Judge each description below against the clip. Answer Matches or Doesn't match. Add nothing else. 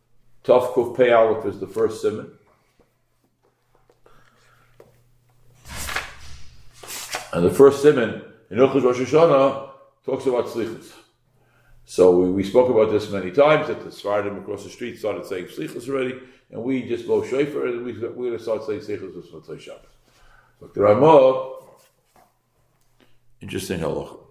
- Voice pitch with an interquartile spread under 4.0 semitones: Doesn't match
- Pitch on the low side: Matches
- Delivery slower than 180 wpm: Matches